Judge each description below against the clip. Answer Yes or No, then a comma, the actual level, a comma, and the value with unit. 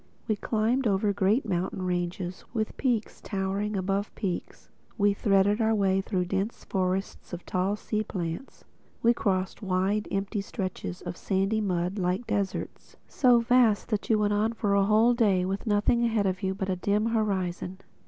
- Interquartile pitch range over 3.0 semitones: No, narrow, 2.4 semitones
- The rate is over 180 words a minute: No, average, 165 wpm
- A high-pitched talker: Yes, high, 200 Hz